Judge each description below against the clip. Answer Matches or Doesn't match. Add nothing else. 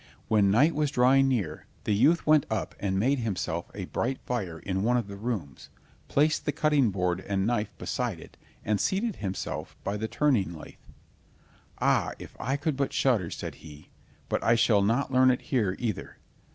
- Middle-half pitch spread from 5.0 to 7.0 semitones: Matches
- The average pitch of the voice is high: Doesn't match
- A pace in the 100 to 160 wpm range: Doesn't match